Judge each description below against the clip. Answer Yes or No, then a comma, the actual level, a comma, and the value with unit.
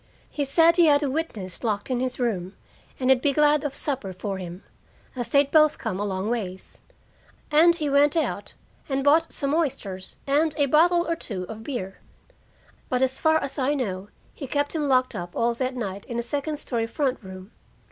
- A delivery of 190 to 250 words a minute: Yes, average, 200 wpm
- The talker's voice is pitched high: Yes, very high, 260 Hz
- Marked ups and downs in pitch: Yes, wide, 6.0 semitones